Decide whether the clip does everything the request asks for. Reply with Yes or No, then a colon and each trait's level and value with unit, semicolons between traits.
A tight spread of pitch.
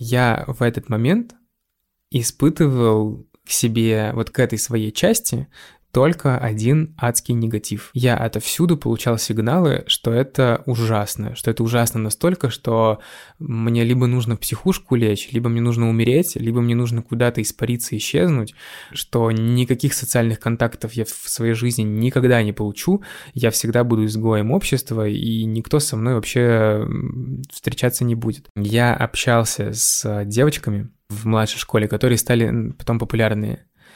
Yes: narrow, 2.3 semitones